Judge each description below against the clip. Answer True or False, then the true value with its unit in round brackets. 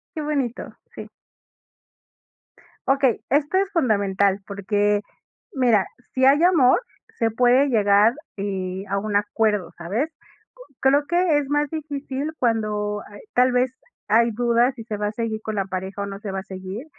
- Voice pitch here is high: True (225 Hz)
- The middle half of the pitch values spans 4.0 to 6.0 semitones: True (4.9 semitones)